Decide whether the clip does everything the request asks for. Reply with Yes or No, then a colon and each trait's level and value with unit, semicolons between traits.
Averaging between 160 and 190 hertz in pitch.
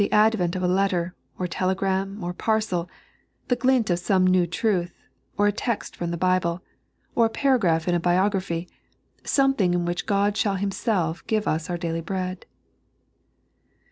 Yes: medium, 185 Hz